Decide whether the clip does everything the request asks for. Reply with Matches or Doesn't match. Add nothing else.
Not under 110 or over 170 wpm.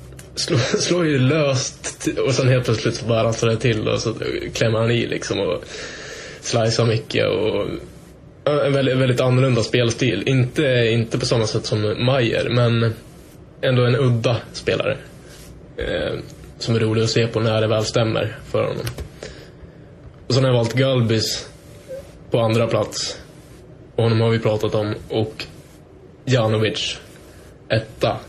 Matches